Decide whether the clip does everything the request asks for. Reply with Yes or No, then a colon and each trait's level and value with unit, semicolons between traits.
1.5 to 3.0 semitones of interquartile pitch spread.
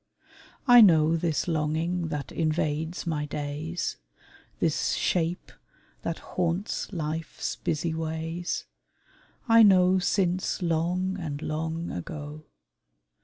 Yes: narrow, 2.5 semitones